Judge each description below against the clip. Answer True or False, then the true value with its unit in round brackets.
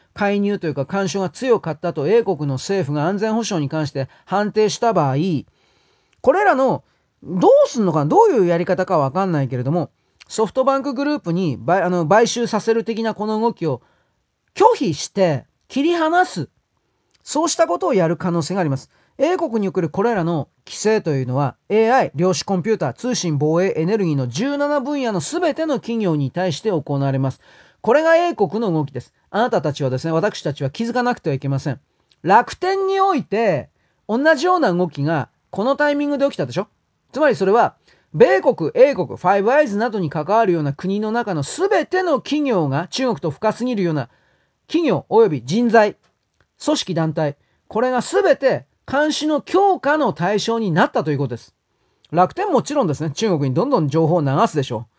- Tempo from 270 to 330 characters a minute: False (365 characters per minute)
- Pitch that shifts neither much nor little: False (8.0 semitones)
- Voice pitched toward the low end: False (195 Hz)